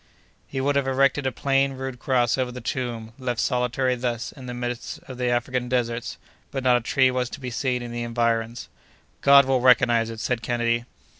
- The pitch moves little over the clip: Yes, narrow, 1.7 semitones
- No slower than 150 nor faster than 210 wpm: Yes, fast, 205 wpm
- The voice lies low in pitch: Yes, low, 125 Hz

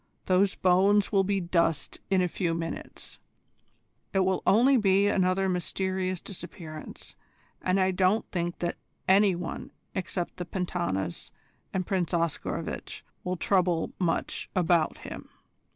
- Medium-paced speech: No, slow, 130 wpm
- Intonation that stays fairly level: Yes, narrow, 1.9 semitones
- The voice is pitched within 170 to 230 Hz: Yes, medium, 185 Hz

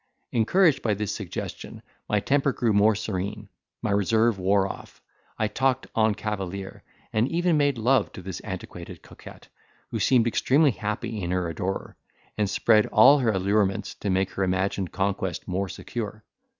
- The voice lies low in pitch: Yes, low, 105 Hz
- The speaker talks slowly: No, average, 160 wpm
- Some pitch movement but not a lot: Yes, average, 3.3 semitones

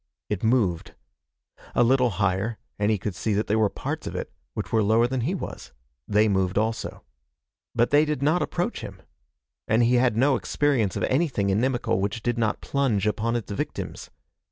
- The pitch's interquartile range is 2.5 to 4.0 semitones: Yes, average, 3.4 semitones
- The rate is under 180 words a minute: No, average, 185 wpm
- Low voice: Yes, low, 115 Hz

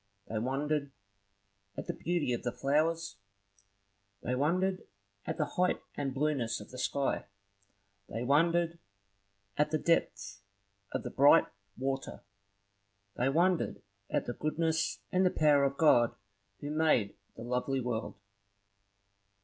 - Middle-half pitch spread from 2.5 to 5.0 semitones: Yes, average, 4.4 semitones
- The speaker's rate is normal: No, slow, 130 wpm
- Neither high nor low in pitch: Yes, medium, 145 Hz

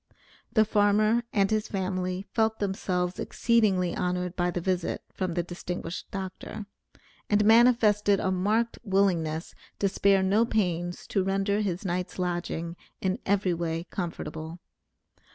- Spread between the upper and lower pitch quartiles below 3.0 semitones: Yes, narrow, 2.6 semitones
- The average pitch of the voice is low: No, high, 190 Hz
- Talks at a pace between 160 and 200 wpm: No, slow, 135 wpm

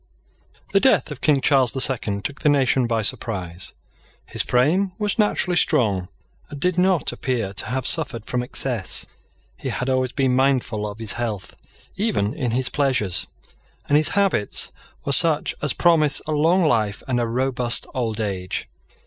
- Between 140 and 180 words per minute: Yes, average, 165 wpm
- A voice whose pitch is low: Yes, low, 130 Hz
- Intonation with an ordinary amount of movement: Yes, average, 5.0 semitones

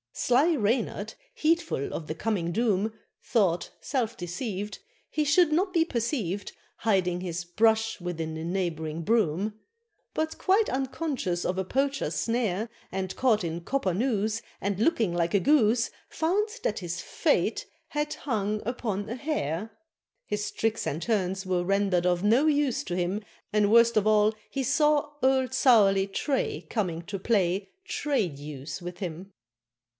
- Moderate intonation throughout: No, wide, 6.1 semitones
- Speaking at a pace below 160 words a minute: Yes, average, 150 wpm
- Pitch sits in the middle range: No, high, 210 Hz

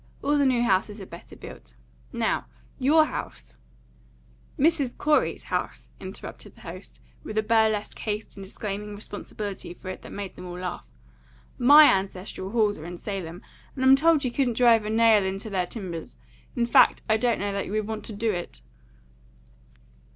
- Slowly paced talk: No, average, 180 wpm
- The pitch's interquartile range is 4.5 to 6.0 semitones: No, average, 4.0 semitones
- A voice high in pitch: Yes, high, 210 Hz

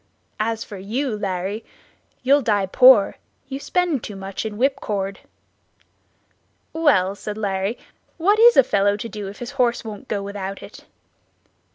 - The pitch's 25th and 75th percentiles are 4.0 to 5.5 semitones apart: Yes, average, 4.7 semitones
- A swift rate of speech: No, average, 150 wpm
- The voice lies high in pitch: Yes, high, 215 Hz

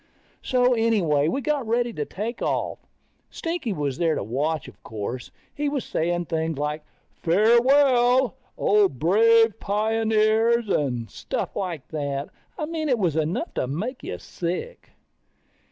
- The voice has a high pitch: Yes, high, 210 Hz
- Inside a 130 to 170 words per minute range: Yes, average, 140 wpm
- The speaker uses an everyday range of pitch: No, wide, 7.5 semitones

